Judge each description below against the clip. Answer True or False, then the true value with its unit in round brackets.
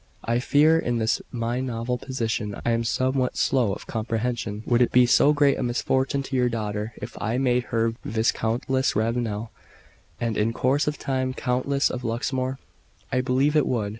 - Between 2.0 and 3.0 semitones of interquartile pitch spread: True (2.4 semitones)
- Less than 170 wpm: False (175 wpm)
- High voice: False (125 Hz)